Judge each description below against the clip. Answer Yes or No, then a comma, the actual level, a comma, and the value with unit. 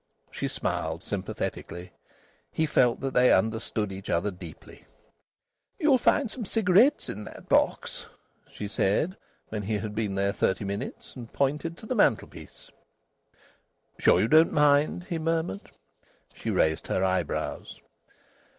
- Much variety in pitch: Yes, wide, 8.7 semitones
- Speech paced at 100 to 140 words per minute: Yes, slow, 135 wpm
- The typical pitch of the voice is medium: No, low, 120 Hz